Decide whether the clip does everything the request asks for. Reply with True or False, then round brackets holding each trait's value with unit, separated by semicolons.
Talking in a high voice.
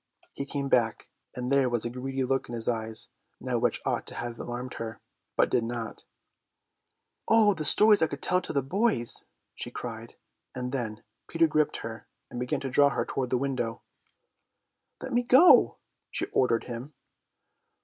False (130 Hz)